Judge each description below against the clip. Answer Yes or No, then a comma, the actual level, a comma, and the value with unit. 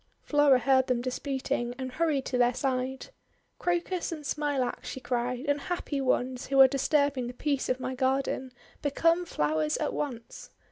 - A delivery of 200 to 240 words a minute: No, average, 155 wpm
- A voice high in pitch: Yes, very high, 265 Hz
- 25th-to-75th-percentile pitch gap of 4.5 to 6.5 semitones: No, narrow, 2.4 semitones